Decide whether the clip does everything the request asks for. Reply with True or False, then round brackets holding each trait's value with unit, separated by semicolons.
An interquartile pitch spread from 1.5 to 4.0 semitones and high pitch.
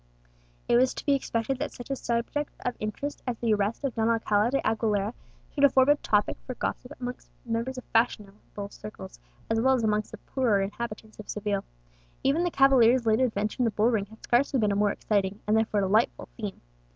True (3.3 semitones; 225 Hz)